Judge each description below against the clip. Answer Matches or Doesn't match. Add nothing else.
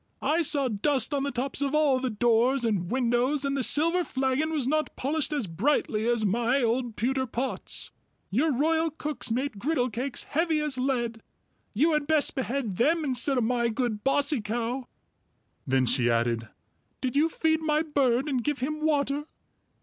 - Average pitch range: Matches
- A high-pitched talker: Matches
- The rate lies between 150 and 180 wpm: Matches